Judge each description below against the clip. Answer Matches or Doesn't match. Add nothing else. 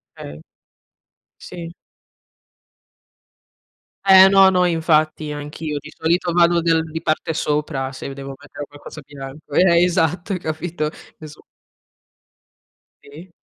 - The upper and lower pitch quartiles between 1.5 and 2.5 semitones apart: Doesn't match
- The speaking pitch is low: Doesn't match